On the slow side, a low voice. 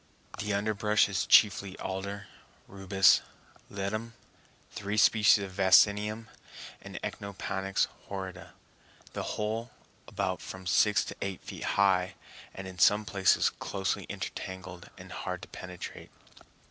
Yes: slow, 120 wpm; low, 100 Hz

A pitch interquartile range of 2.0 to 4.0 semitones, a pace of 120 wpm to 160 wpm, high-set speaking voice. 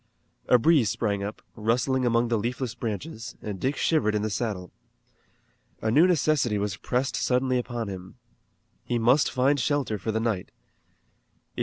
No: average, 3.6 semitones; average, 155 wpm; low, 120 Hz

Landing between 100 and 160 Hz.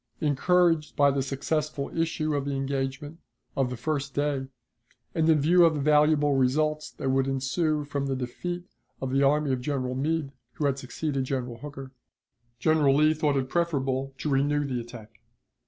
Yes: medium, 140 Hz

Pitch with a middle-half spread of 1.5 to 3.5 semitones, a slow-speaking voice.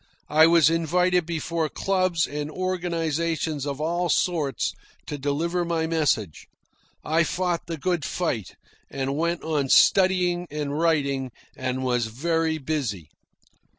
Yes: average, 3.2 semitones; slow, 125 wpm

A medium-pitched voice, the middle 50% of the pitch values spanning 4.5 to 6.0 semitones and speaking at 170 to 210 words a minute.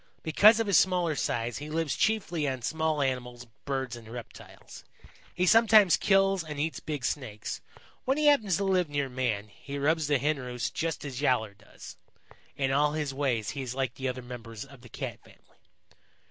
Yes: medium, 145 Hz; average, 4.8 semitones; average, 190 wpm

